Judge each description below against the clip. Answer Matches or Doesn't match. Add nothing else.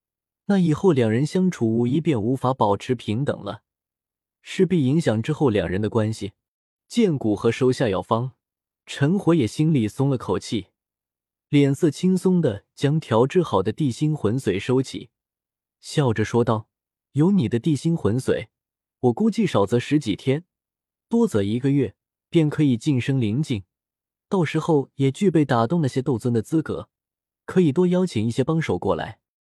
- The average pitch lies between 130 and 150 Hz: Matches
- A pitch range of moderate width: Doesn't match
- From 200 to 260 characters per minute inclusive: Matches